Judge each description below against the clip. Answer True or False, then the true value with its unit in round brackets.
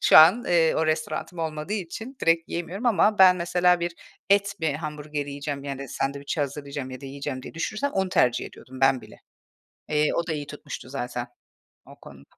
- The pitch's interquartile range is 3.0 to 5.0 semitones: True (4.0 semitones)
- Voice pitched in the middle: True (155 Hz)